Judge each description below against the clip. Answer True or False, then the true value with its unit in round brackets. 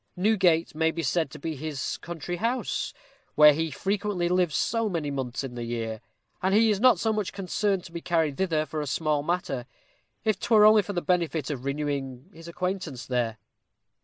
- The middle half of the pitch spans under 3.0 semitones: False (5.1 semitones)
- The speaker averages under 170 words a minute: False (190 wpm)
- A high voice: False (165 Hz)